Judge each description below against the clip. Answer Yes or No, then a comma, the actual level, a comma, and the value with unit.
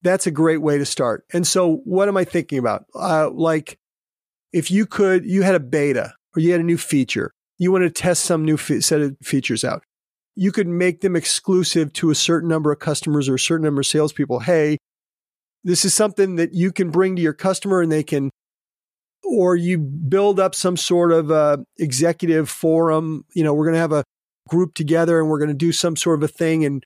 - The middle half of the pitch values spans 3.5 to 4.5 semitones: No, average, 3.0 semitones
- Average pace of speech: No, fast, 220 wpm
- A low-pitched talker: No, medium, 165 Hz